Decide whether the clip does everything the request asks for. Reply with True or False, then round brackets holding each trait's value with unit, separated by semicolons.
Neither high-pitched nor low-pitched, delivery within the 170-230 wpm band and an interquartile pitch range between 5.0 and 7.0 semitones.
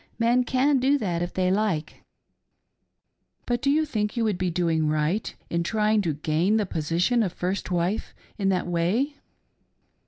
False (195 Hz; 175 wpm; 5.4 semitones)